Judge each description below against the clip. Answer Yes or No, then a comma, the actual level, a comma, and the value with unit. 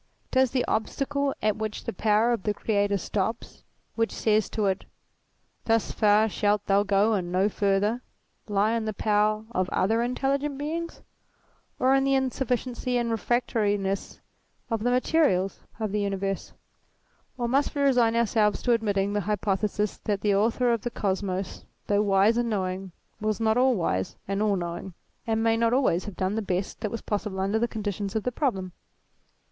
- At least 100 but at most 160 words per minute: No, average, 175 wpm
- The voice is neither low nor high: No, high, 215 Hz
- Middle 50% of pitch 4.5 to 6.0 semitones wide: No, average, 3.1 semitones